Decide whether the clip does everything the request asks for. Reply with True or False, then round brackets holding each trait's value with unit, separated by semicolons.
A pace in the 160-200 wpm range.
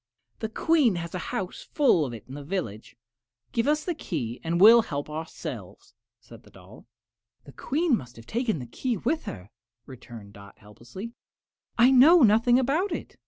True (180 wpm)